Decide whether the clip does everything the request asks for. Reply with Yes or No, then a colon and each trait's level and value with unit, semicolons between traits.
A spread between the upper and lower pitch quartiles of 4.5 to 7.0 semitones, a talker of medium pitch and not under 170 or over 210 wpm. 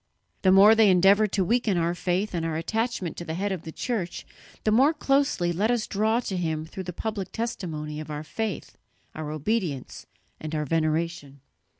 Yes: average, 5.3 semitones; medium, 180 Hz; average, 190 wpm